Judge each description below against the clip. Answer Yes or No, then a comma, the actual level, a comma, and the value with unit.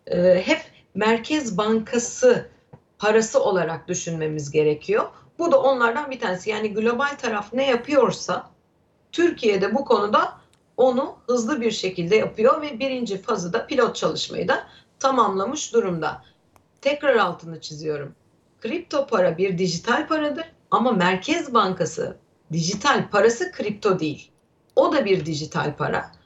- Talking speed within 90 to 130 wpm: Yes, average, 125 wpm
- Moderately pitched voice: No, high, 225 Hz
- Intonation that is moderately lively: No, wide, 7.1 semitones